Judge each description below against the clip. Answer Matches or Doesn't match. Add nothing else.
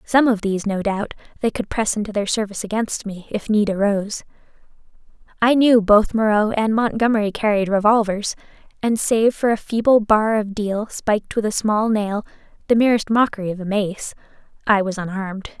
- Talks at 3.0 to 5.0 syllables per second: Doesn't match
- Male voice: Doesn't match